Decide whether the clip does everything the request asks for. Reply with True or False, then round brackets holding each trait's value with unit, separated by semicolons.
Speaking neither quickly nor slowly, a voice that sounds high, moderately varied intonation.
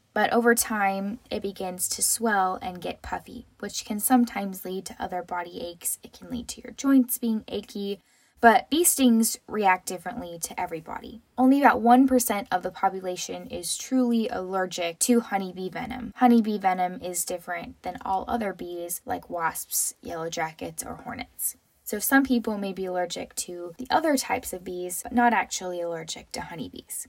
True (170 wpm; 205 Hz; 4.9 semitones)